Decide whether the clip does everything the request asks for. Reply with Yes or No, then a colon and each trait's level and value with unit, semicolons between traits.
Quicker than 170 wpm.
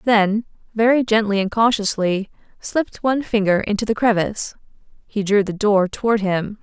No: average, 155 wpm